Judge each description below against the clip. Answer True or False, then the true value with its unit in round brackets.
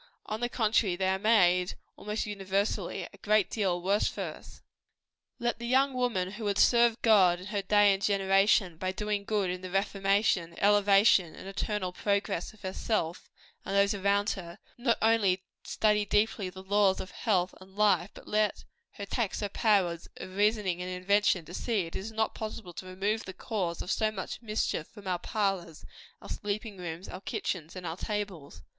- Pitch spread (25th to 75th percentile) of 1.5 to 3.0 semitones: True (2.5 semitones)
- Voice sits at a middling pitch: False (200 Hz)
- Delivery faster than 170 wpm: True (185 wpm)